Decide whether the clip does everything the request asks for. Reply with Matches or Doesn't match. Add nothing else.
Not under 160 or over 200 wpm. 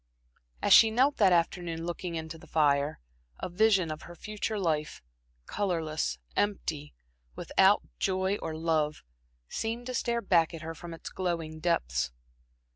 Doesn't match